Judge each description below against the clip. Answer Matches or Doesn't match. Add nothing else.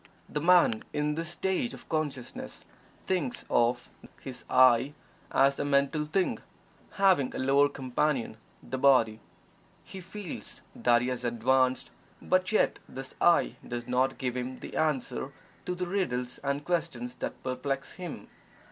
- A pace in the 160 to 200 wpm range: Doesn't match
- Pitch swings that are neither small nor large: Matches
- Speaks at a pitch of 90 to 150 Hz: Matches